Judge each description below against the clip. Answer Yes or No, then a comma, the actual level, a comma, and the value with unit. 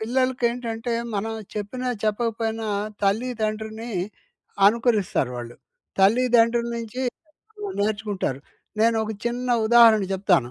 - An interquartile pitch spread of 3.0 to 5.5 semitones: No, narrow, 2.4 semitones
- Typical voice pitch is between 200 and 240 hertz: Yes, high, 225 Hz